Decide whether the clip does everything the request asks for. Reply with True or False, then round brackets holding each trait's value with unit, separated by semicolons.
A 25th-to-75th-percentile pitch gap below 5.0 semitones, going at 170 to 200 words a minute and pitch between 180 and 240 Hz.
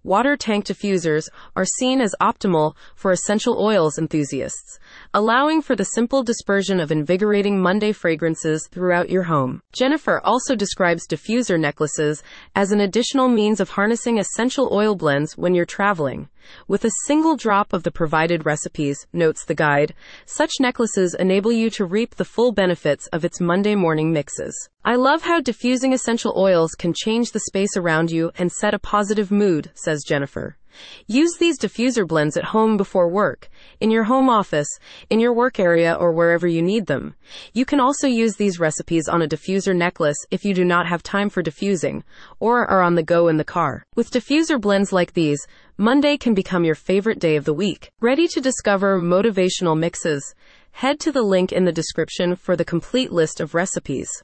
False (5.3 semitones; 180 wpm; 190 Hz)